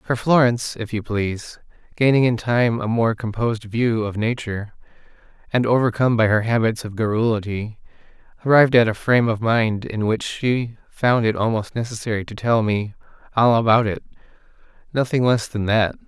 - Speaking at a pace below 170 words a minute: Yes, average, 160 wpm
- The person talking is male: Yes, male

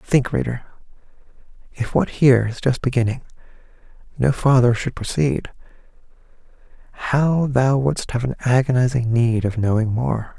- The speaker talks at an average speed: No, slow, 125 wpm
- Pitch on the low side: Yes, low, 125 Hz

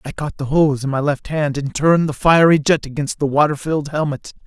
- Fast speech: Yes, fast, 240 wpm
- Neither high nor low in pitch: Yes, medium, 145 Hz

